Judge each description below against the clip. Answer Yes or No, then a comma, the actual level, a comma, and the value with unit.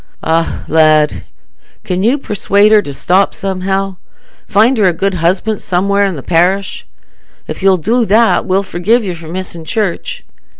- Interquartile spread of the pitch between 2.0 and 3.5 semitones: Yes, average, 2.8 semitones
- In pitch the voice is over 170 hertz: Yes, high, 190 Hz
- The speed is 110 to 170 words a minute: Yes, average, 160 wpm